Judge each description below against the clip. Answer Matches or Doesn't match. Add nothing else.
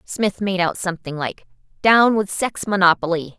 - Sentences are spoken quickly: Doesn't match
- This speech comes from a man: Doesn't match